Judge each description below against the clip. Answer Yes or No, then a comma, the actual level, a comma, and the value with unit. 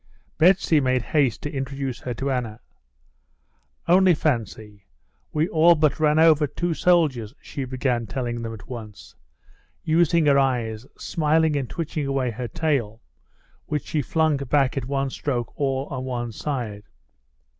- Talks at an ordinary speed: Yes, average, 145 wpm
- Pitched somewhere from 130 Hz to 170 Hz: Yes, low, 135 Hz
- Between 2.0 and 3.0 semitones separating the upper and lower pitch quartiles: No, average, 4.2 semitones